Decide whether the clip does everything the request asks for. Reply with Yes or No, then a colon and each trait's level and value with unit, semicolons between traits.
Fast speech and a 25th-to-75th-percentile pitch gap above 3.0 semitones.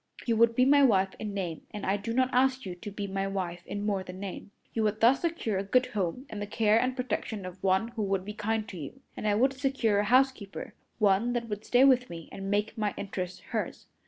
Yes: fast, 245 wpm; average, 4.0 semitones